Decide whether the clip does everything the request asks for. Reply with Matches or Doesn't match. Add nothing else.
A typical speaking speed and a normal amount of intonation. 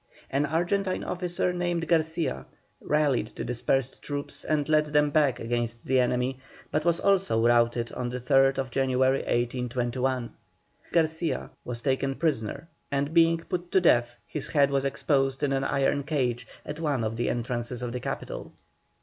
Matches